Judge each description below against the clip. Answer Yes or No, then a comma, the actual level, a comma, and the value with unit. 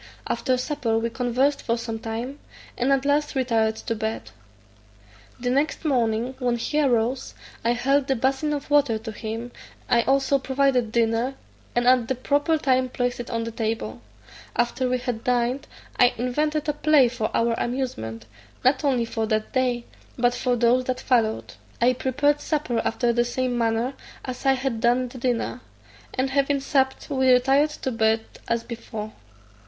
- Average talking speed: Yes, average, 170 wpm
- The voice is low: No, very high, 250 Hz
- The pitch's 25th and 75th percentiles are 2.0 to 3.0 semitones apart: Yes, narrow, 2.6 semitones